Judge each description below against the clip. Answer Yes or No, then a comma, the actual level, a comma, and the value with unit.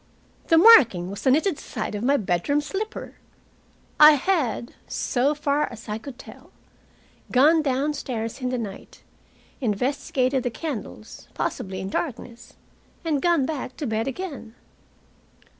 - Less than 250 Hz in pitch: No, very high, 260 Hz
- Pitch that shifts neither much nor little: Yes, average, 4.9 semitones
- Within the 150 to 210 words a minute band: No, slow, 135 wpm